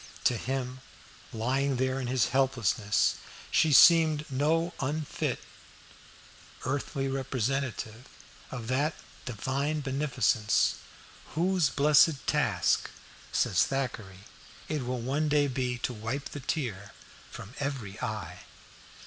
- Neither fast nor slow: No, slow, 105 wpm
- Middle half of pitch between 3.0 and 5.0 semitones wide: Yes, average, 3.3 semitones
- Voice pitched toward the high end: No, low, 130 Hz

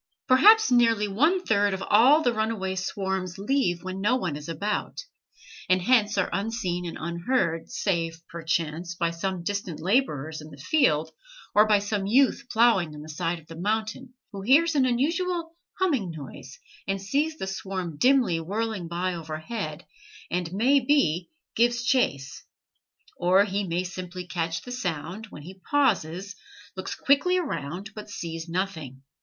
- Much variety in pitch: Yes, wide, 6.0 semitones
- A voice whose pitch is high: Yes, high, 195 Hz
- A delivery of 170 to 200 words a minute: No, average, 155 wpm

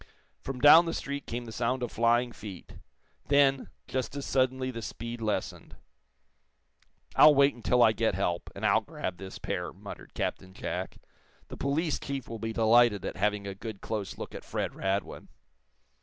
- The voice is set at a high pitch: No, low, 115 Hz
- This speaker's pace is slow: No, average, 170 wpm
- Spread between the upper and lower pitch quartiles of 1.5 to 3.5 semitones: No, average, 4.3 semitones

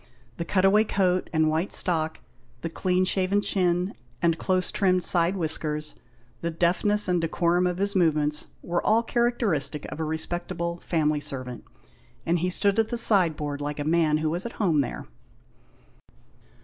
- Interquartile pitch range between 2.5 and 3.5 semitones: Yes, average, 3.2 semitones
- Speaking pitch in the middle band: Yes, medium, 175 Hz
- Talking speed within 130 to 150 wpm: No, average, 160 wpm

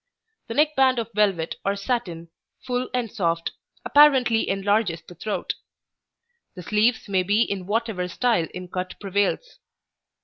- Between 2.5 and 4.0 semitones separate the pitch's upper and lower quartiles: No, average, 4.8 semitones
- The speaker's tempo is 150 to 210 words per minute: No, average, 140 wpm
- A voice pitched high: Yes, high, 205 Hz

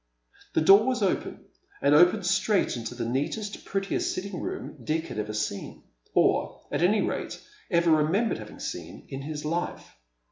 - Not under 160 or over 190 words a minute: Yes, average, 175 wpm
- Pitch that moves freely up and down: Yes, wide, 7.9 semitones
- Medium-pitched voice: Yes, medium, 160 Hz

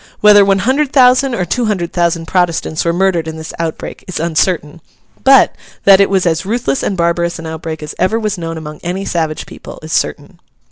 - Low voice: No, medium, 175 Hz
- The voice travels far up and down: No, average, 3.4 semitones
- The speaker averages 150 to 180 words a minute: No, average, 200 wpm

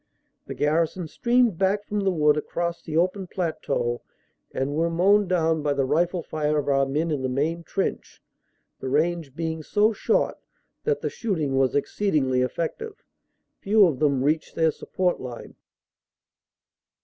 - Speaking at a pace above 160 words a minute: No, average, 155 wpm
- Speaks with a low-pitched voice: No, medium, 160 Hz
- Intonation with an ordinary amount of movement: Yes, average, 4.4 semitones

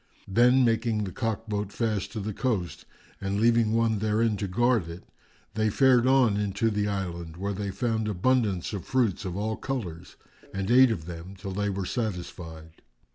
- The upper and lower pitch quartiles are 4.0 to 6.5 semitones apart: No, average, 3.3 semitones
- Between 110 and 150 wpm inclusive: No, average, 180 wpm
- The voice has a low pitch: Yes, low, 105 Hz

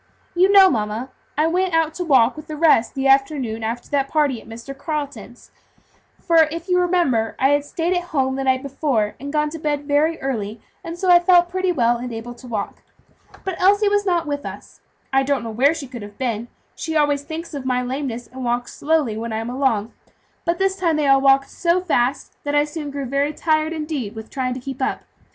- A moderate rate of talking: No, fast, 225 wpm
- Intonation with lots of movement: No, average, 4.7 semitones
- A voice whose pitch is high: Yes, very high, 285 Hz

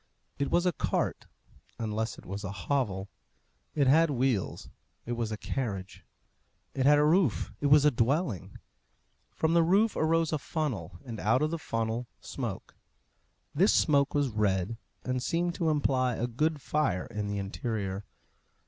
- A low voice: Yes, low, 130 Hz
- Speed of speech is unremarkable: Yes, average, 160 wpm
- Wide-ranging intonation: Yes, wide, 6.1 semitones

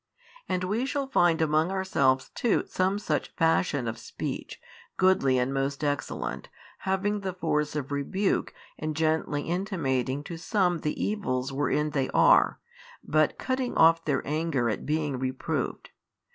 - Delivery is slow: No, average, 145 wpm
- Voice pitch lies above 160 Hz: No, medium, 155 Hz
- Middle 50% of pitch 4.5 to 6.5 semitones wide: Yes, average, 5.2 semitones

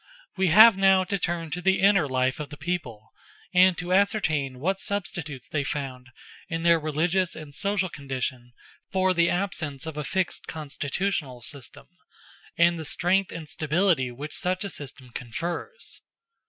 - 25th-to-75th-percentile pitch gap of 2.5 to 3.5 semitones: No, average, 5.0 semitones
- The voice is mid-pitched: Yes, medium, 165 Hz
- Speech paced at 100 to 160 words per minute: Yes, average, 155 wpm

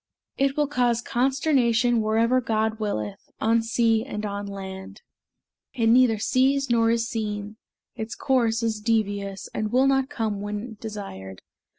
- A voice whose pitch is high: Yes, high, 225 Hz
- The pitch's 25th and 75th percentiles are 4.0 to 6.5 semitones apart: No, average, 2.9 semitones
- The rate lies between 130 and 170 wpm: Yes, average, 145 wpm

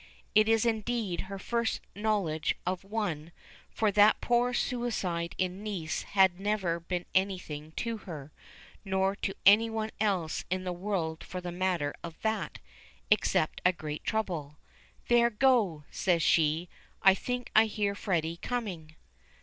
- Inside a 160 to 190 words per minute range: No, average, 145 wpm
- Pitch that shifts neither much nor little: Yes, average, 4.4 semitones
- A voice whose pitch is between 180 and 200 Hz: Yes, high, 190 Hz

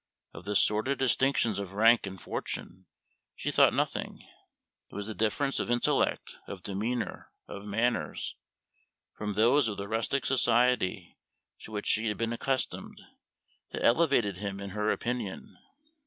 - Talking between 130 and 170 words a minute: Yes, average, 145 wpm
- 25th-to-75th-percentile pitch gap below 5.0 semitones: Yes, average, 3.4 semitones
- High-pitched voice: No, low, 110 Hz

